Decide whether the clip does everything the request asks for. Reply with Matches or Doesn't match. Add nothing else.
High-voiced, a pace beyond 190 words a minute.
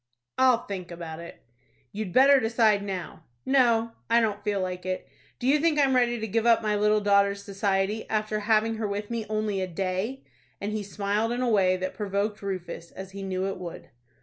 Matches